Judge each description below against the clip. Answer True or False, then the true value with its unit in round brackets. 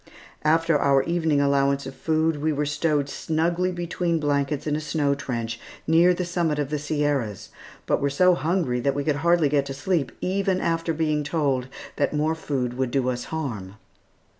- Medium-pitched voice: True (150 Hz)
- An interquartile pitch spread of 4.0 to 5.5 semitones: False (2.9 semitones)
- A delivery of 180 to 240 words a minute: True (185 wpm)